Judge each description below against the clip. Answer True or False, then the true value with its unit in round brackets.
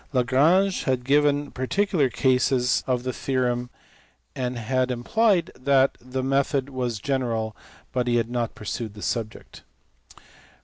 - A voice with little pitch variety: True (2.2 semitones)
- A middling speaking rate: False (130 wpm)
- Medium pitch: False (130 Hz)